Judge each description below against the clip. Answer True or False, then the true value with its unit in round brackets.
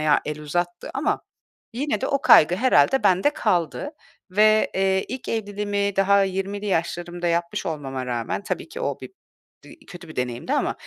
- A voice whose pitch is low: False (190 Hz)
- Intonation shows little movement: False (3.9 semitones)